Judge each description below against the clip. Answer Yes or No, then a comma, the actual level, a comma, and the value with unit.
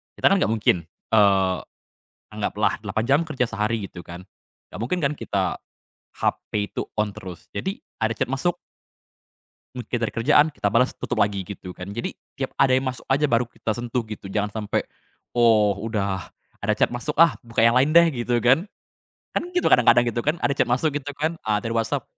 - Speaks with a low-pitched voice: Yes, low, 115 Hz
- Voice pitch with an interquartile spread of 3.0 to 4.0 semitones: No, average, 4.4 semitones